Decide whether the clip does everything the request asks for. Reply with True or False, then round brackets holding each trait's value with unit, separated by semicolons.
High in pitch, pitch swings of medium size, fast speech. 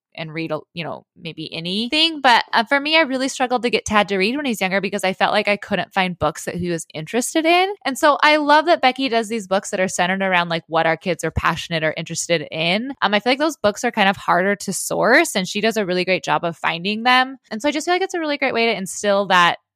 False (205 Hz; 6.7 semitones; 280 wpm)